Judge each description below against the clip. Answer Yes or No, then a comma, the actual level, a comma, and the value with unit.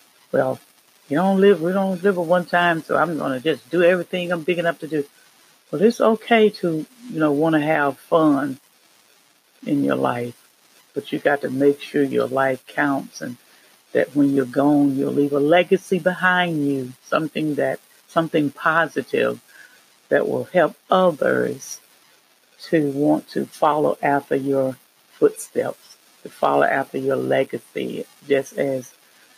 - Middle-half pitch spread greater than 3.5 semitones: Yes, average, 4.4 semitones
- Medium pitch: Yes, medium, 155 Hz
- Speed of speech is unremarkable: Yes, average, 155 wpm